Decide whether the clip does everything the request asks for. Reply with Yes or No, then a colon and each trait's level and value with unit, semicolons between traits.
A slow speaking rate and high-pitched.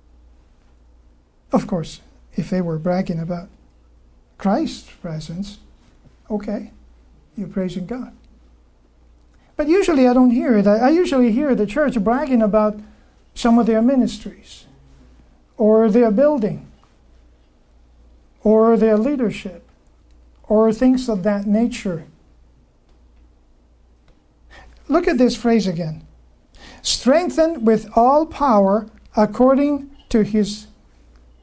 Yes: slow, 100 wpm; high, 200 Hz